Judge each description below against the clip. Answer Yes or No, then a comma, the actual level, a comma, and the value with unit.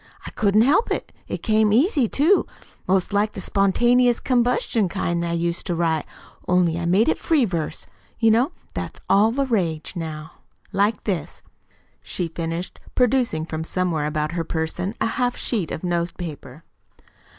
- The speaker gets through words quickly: No, average, 170 wpm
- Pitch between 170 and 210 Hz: Yes, high, 190 Hz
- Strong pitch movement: Yes, wide, 5.7 semitones